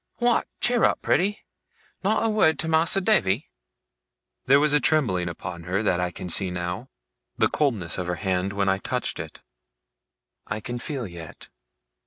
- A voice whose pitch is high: No, low, 105 Hz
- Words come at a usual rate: Yes, average, 170 wpm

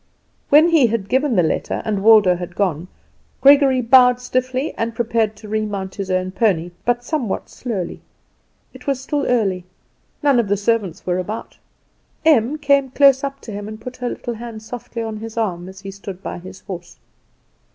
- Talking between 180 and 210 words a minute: Yes, average, 185 wpm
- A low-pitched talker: No, high, 225 Hz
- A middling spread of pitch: Yes, average, 4.6 semitones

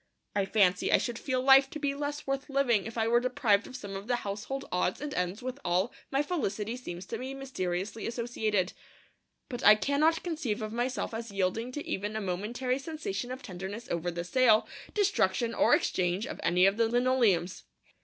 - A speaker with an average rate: Yes, average, 195 wpm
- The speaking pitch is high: Yes, high, 230 Hz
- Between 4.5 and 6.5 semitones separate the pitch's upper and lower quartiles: Yes, average, 5.2 semitones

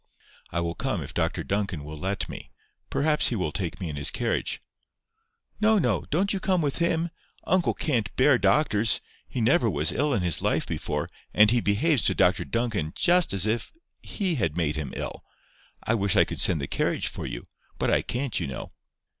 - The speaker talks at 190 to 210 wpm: Yes, average, 200 wpm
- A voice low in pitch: Yes, low, 110 Hz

